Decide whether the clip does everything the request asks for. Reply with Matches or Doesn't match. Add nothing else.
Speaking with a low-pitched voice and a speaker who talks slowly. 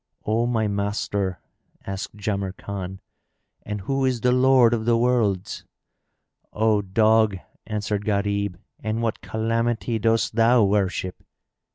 Matches